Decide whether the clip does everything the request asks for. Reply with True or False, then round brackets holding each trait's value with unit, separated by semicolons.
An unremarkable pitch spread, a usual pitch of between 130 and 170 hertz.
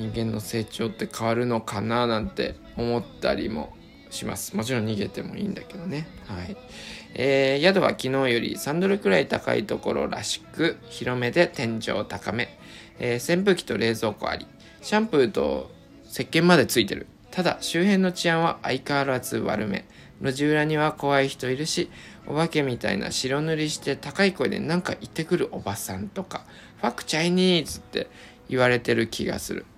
False (6.4 semitones; 135 Hz)